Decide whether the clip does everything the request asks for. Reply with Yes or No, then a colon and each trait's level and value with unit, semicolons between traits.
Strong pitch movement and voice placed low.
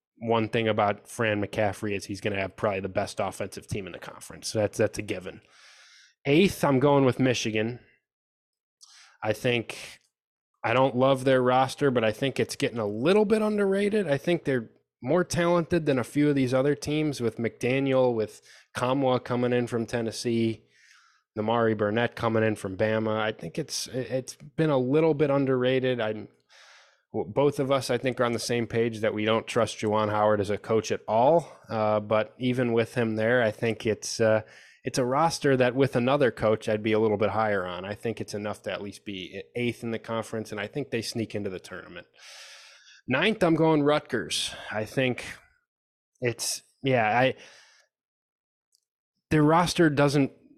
No: average, 4.0 semitones; low, 120 Hz